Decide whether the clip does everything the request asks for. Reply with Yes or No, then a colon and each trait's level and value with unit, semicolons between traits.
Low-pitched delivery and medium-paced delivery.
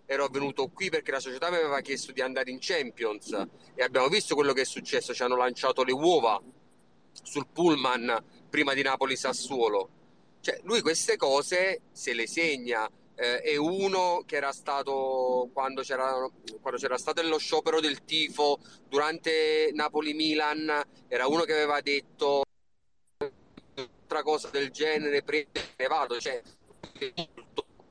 No: medium, 145 Hz; average, 145 wpm